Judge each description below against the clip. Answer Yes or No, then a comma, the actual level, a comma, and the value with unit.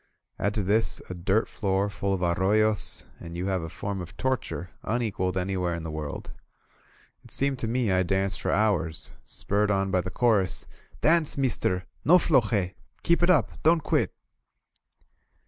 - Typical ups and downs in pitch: Yes, average, 3.8 semitones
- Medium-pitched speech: No, low, 100 Hz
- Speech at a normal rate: Yes, average, 170 wpm